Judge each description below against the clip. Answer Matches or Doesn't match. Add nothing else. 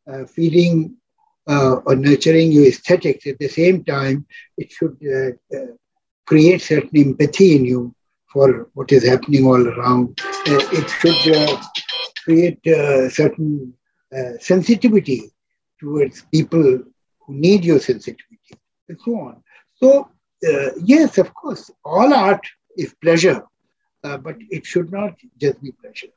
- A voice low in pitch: Doesn't match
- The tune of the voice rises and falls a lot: Matches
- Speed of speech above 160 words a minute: Doesn't match